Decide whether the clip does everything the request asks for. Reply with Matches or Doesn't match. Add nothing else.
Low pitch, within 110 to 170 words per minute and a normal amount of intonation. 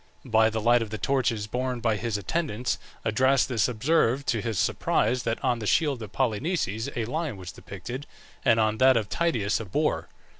Doesn't match